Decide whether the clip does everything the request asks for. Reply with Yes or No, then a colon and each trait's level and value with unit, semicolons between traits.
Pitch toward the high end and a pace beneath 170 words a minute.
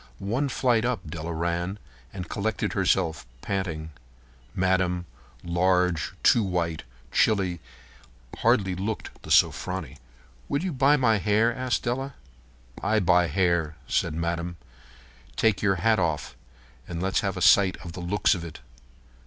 No: very low, 95 Hz; slow, 135 wpm